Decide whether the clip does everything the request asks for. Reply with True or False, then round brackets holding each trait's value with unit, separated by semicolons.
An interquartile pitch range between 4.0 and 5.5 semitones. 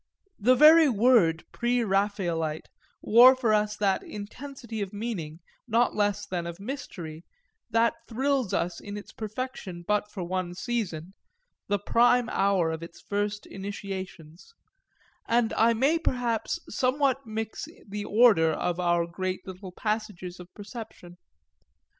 True (4.5 semitones)